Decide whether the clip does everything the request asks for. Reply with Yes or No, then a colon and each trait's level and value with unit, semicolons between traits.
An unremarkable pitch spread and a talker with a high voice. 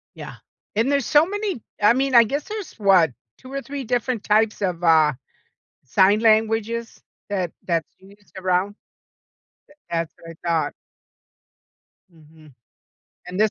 No: wide, 6.1 semitones; high, 210 Hz